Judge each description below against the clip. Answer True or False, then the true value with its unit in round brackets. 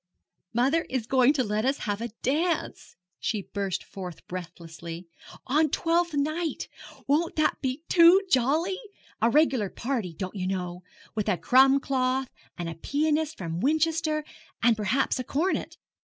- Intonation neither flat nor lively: False (7.4 semitones)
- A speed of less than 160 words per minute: True (150 wpm)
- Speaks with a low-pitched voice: False (260 Hz)